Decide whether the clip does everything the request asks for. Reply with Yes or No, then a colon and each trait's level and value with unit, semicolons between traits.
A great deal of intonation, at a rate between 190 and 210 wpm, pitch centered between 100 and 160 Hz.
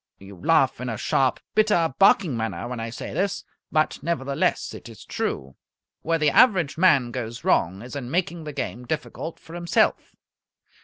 No: wide, 6.0 semitones; average, 170 wpm; medium, 140 Hz